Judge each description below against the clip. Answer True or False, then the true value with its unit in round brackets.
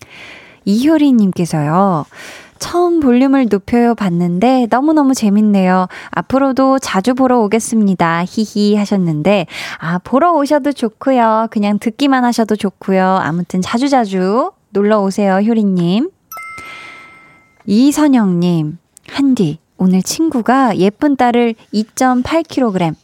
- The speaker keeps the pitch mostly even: False (5.6 semitones)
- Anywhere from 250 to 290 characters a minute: True (255 characters per minute)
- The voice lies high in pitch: True (225 Hz)